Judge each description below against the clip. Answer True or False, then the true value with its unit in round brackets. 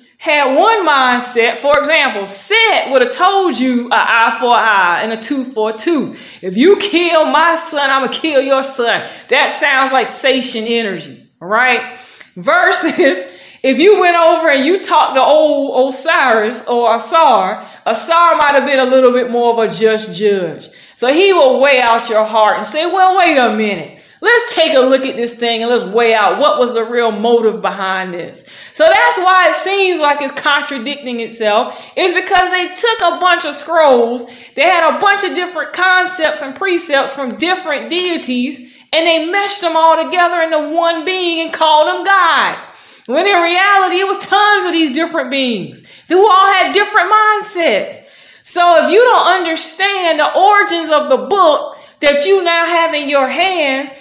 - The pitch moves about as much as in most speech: False (6.0 semitones)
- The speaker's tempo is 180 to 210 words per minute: True (185 wpm)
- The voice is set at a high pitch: True (300 Hz)